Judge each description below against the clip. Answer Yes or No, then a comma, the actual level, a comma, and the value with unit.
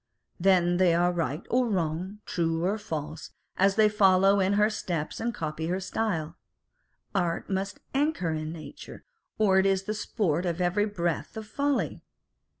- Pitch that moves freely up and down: No, average, 3.8 semitones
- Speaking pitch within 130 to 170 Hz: No, medium, 185 Hz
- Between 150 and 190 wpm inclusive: Yes, average, 160 wpm